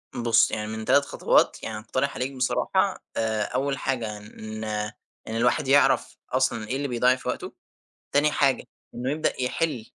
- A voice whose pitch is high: No, low, 125 Hz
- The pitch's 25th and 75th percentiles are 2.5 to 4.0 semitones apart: Yes, average, 3.6 semitones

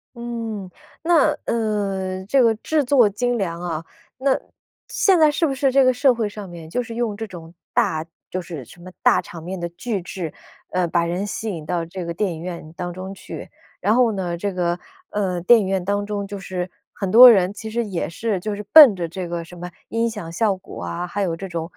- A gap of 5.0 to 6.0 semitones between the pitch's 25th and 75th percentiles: No, average, 4.6 semitones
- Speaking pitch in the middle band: No, high, 195 Hz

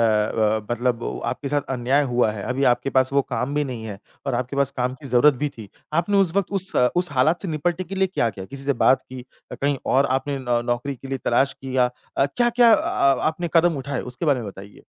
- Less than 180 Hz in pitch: Yes, low, 135 Hz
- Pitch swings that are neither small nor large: Yes, average, 3.4 semitones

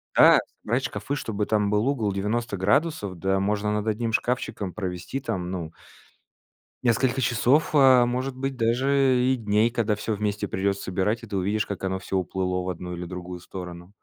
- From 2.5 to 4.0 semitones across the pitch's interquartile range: No, average, 4.4 semitones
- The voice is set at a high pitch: No, low, 105 Hz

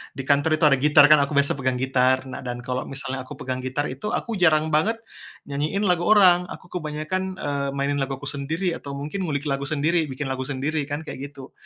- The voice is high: No, medium, 145 Hz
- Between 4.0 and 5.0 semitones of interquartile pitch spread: No, average, 2.8 semitones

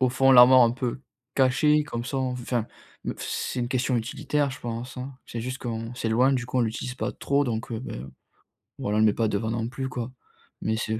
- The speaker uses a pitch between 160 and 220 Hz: No, low, 125 Hz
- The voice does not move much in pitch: Yes, narrow, 2.3 semitones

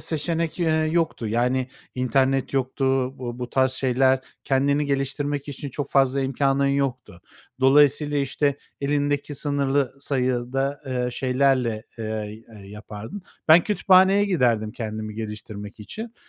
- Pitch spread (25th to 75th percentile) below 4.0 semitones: Yes, average, 2.8 semitones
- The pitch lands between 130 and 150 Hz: Yes, low, 135 Hz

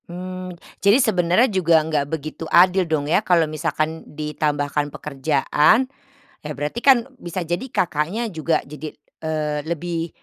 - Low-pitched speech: No, medium, 160 Hz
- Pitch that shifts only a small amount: No, average, 3.3 semitones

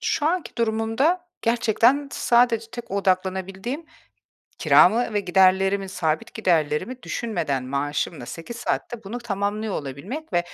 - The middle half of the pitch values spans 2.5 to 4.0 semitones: No, average, 4.8 semitones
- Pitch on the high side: Yes, high, 205 Hz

